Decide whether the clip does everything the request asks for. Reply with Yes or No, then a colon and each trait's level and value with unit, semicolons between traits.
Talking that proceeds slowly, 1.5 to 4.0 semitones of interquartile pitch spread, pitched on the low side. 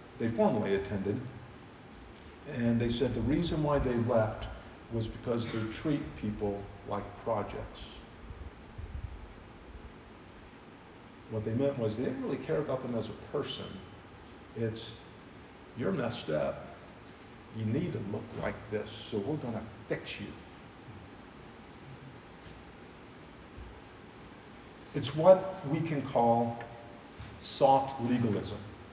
Yes: slow, 110 wpm; average, 3.1 semitones; low, 115 Hz